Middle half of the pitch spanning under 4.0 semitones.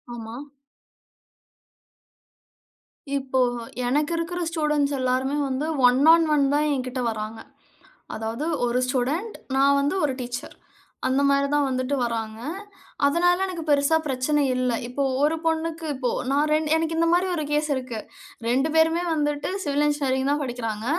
Yes: average, 3.4 semitones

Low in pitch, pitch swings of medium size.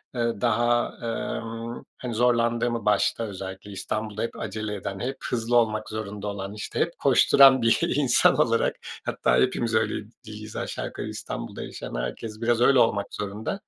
No: low, 115 Hz; narrow, 2.3 semitones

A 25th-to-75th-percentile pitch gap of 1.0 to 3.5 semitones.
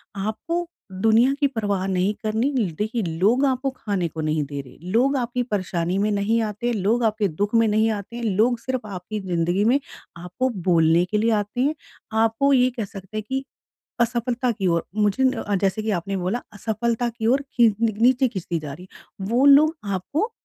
No: average, 4.1 semitones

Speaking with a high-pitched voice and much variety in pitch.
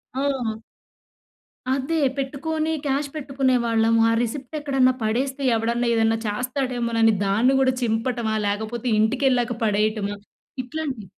No: high, 245 Hz; average, 3.2 semitones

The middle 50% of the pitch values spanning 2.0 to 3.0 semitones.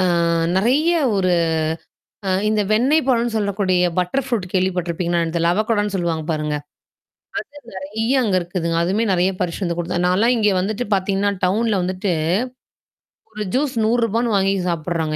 No: average, 4.0 semitones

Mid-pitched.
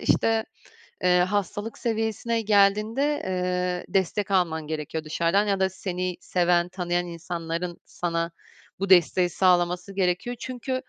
Yes: medium, 180 Hz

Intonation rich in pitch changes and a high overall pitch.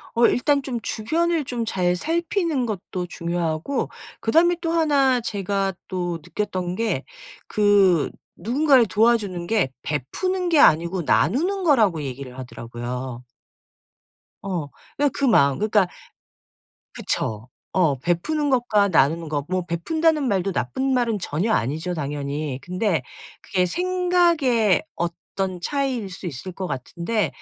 Yes: wide, 7.9 semitones; high, 195 Hz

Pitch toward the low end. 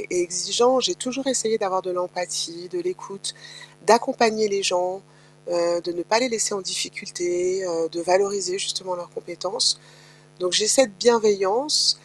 No: high, 190 Hz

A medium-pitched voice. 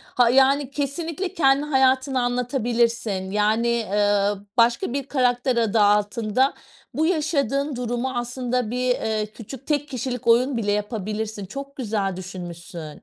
No: high, 240 Hz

